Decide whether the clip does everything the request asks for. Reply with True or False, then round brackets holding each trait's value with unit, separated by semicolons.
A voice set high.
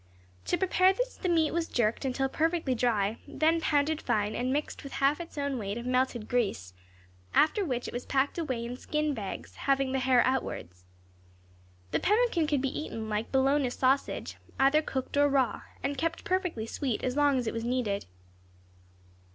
True (270 Hz)